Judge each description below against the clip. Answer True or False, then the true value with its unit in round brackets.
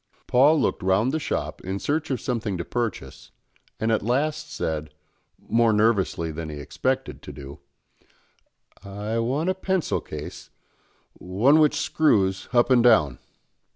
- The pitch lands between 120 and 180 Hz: False (110 Hz)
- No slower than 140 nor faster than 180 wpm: True (145 wpm)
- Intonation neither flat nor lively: False (7.1 semitones)